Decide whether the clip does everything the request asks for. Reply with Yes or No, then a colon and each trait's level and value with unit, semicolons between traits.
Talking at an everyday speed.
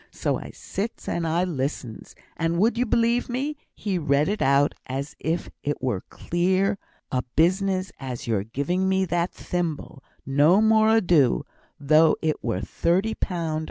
Yes: average, 160 wpm